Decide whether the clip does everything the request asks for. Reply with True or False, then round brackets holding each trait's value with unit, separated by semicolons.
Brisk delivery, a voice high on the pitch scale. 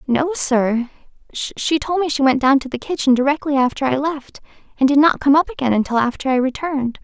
True (215 wpm; 275 Hz)